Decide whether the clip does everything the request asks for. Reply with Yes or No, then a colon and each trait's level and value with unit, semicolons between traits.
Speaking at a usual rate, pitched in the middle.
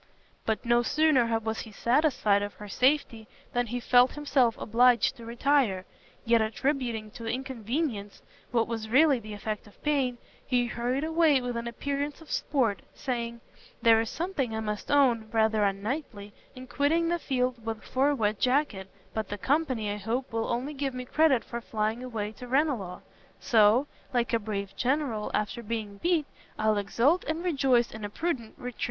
No: average, 170 wpm; high, 240 Hz